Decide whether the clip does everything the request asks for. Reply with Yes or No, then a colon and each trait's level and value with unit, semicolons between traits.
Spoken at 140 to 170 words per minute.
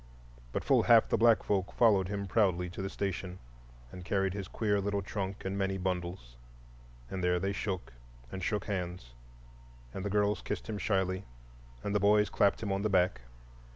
No: average, 185 wpm